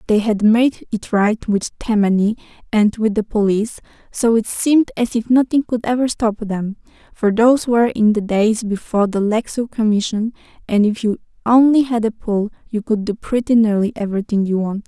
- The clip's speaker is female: Yes, female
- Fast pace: No, average, 185 wpm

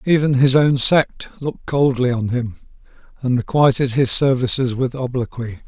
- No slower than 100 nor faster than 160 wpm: Yes, average, 150 wpm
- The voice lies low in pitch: Yes, low, 130 Hz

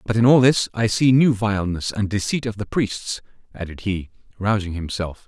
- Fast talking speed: No, average, 195 wpm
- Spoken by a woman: No, male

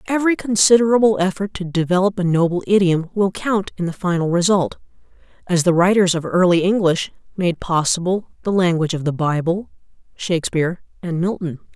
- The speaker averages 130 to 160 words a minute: Yes, average, 155 wpm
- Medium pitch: Yes, medium, 180 Hz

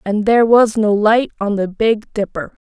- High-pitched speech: Yes, high, 215 Hz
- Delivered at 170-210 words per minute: Yes, average, 200 wpm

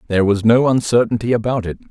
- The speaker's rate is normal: Yes, average, 190 wpm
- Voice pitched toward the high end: No, low, 115 Hz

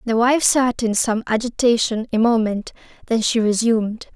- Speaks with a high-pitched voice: Yes, high, 230 Hz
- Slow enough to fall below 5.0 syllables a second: Yes, 4.8 syllables/s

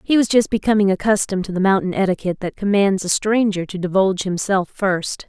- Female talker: Yes, female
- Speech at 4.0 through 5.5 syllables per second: No, 6.0 syllables/s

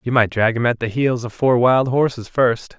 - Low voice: Yes, low, 120 Hz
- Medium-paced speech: No, fast, 260 wpm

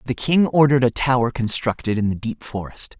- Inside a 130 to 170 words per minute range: No, average, 200 wpm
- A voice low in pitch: Yes, low, 120 Hz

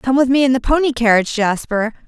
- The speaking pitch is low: No, high, 245 Hz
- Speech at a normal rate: No, fast, 230 wpm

